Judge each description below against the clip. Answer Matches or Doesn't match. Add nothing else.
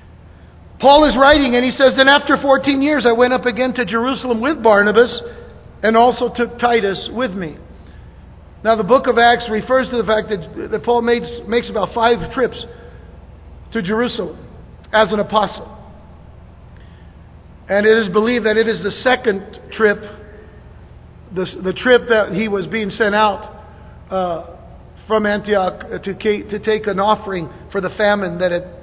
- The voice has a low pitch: Doesn't match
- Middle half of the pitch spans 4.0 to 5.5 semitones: Doesn't match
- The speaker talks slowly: Doesn't match